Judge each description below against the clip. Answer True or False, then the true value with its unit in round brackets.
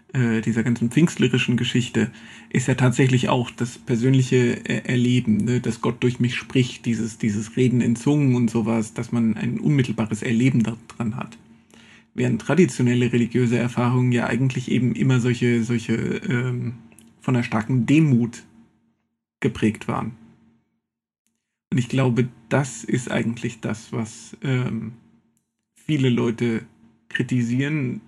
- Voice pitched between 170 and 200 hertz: False (120 Hz)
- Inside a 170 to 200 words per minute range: False (130 wpm)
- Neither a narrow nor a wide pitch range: False (1.7 semitones)